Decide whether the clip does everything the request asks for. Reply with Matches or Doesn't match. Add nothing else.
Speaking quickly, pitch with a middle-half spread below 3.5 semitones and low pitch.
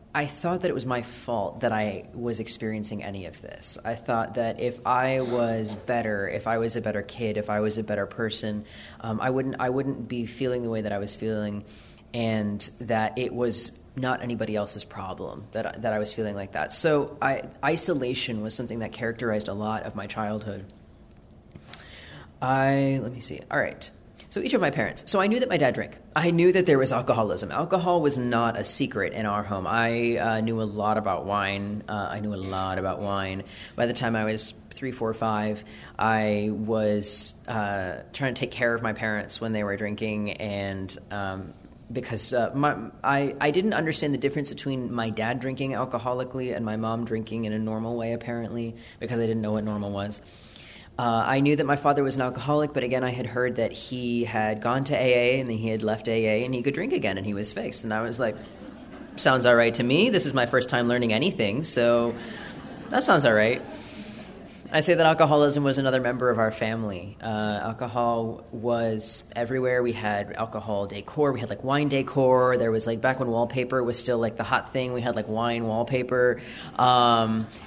Matches